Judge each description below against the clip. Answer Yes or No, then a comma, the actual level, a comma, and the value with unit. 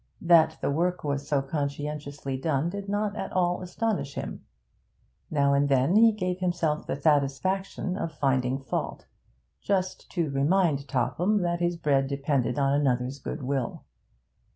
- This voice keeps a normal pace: Yes, average, 145 wpm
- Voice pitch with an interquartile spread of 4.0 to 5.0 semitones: Yes, average, 4.5 semitones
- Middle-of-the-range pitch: Yes, medium, 150 Hz